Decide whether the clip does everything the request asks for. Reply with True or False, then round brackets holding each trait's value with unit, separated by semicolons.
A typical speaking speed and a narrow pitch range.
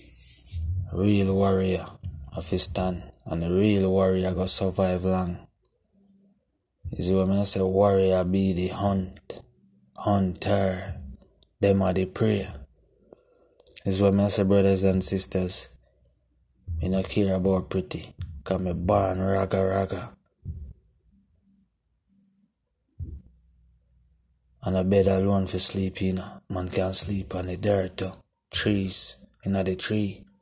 False (120 wpm; 1.5 semitones)